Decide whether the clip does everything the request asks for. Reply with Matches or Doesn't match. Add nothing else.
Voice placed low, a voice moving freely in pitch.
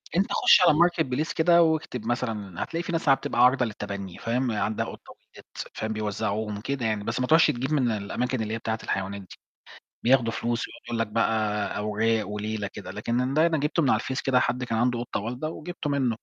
Doesn't match